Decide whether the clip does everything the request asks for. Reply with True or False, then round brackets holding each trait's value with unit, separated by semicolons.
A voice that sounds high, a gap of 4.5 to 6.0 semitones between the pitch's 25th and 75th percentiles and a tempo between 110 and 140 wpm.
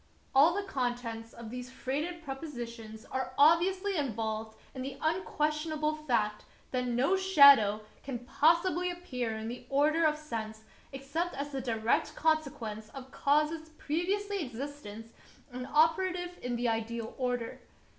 True (275 Hz; 5.3 semitones; 135 wpm)